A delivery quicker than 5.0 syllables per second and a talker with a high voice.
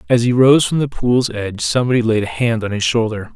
No: 6.0 syllables/s; low, 115 Hz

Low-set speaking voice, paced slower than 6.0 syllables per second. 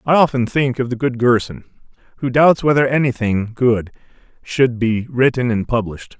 Yes: low, 120 Hz; 5.0 syllables/s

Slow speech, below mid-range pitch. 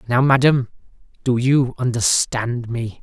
Yes: slow, 120 wpm; low, 125 Hz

